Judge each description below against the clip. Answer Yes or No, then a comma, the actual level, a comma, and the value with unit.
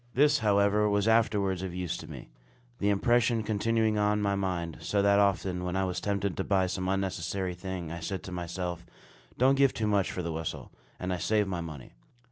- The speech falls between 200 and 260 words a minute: Yes, fast, 205 wpm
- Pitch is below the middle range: Yes, very low, 95 Hz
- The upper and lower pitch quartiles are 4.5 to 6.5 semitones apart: No, narrow, 2.6 semitones